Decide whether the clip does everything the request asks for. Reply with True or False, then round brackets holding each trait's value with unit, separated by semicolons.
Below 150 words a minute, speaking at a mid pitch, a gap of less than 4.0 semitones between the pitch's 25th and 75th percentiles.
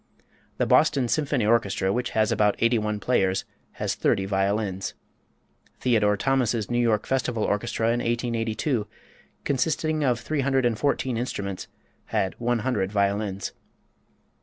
False (135 wpm; 115 Hz; 3.4 semitones)